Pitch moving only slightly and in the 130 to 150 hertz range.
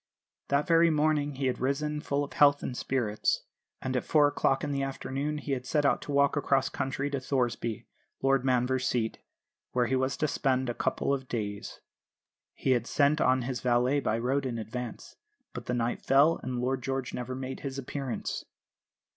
Yes: narrow, 2.2 semitones; low, 135 Hz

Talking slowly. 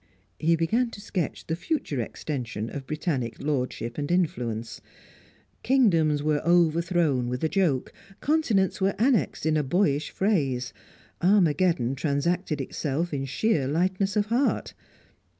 Yes: slow, 130 wpm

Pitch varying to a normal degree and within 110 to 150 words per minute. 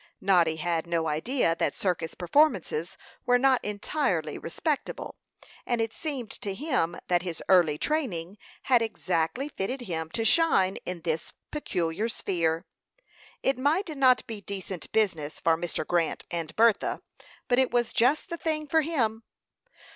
No: wide, 7.6 semitones; average, 145 wpm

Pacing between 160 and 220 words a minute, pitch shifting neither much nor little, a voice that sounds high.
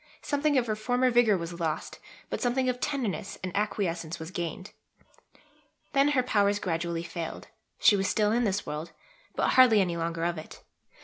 No: average, 175 wpm; wide, 6.3 semitones; high, 200 Hz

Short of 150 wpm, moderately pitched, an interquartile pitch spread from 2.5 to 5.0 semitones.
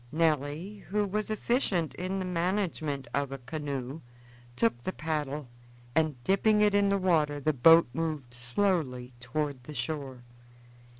No: average, 140 wpm; medium, 155 Hz; wide, 5.4 semitones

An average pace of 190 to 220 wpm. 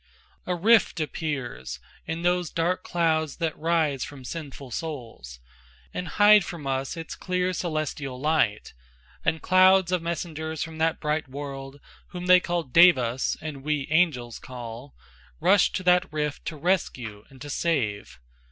No: average, 145 wpm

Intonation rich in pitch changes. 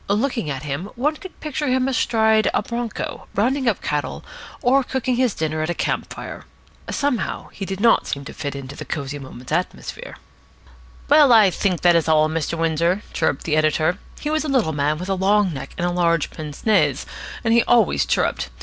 Yes: wide, 7.6 semitones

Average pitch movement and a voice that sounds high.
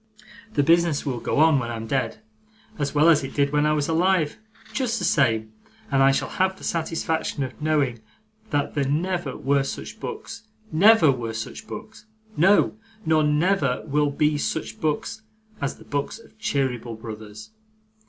No: average, 3.6 semitones; medium, 145 Hz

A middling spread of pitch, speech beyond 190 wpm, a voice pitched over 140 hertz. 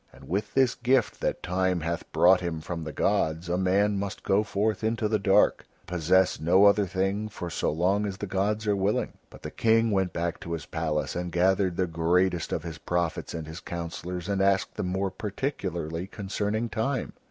No: average, 3.1 semitones; average, 200 wpm; very low, 95 Hz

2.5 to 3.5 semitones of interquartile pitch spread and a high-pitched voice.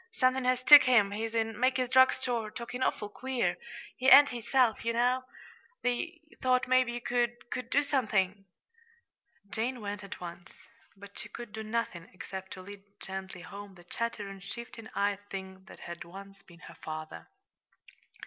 No: average, 4.3 semitones; high, 225 Hz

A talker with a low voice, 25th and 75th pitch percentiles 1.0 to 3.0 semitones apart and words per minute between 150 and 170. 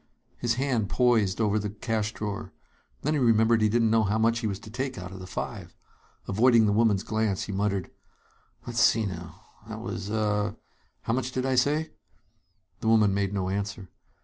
No: low, 110 Hz; narrow, 2.5 semitones; average, 190 wpm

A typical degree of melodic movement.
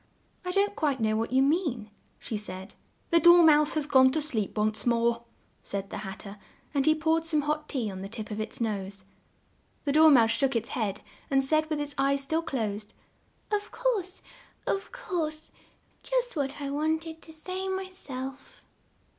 No: wide, 6.2 semitones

